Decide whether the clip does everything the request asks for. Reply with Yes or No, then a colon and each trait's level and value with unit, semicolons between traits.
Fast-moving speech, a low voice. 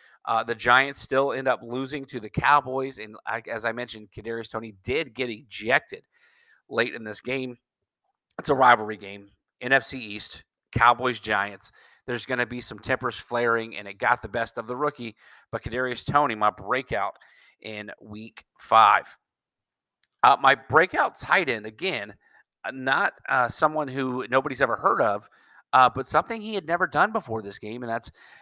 No: average, 170 wpm; low, 120 Hz